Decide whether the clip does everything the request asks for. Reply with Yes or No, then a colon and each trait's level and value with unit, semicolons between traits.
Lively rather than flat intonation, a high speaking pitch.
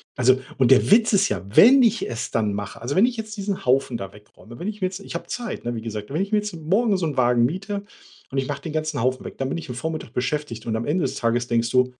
No: wide, 8.4 semitones; medium, 140 Hz